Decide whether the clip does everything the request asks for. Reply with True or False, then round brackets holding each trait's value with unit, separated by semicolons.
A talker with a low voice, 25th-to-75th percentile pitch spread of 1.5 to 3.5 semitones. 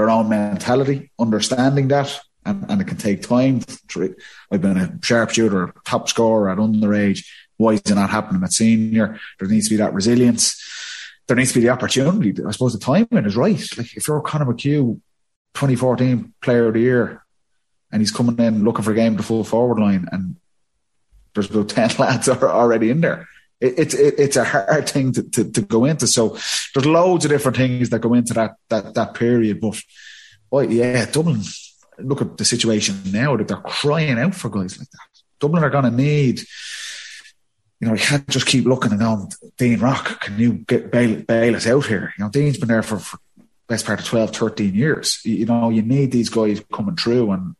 False (120 Hz; 3.9 semitones)